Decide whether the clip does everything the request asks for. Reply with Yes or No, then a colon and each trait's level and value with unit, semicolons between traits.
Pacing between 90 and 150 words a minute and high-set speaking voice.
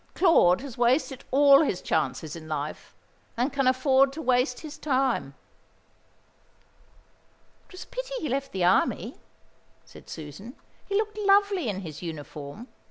Yes: average, 145 wpm; very high, 255 Hz